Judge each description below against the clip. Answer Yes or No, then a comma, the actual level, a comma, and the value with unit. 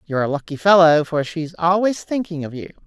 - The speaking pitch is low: No, medium, 165 Hz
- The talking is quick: Yes, fast, 210 wpm